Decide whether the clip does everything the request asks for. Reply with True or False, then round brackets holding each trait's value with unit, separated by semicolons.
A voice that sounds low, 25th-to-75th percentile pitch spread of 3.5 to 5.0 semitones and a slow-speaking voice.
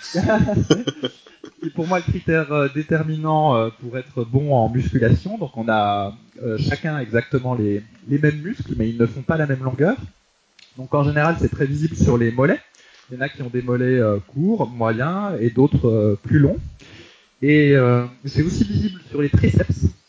False (130 Hz; 4.4 semitones; 175 wpm)